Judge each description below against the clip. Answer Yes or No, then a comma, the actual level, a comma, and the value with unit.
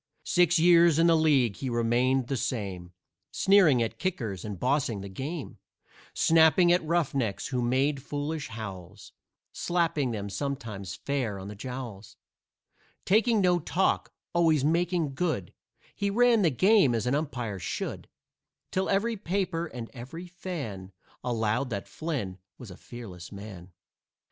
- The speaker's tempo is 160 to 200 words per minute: No, average, 140 wpm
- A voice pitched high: No, low, 135 Hz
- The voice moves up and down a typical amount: No, wide, 7.5 semitones